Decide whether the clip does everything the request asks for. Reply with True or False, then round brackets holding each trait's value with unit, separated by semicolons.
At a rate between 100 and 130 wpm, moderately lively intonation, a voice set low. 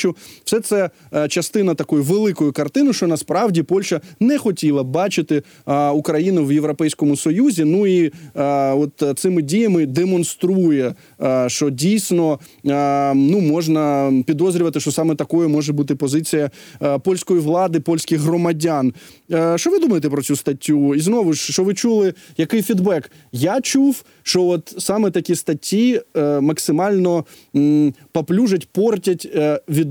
False (125 wpm; 4.1 semitones; 165 Hz)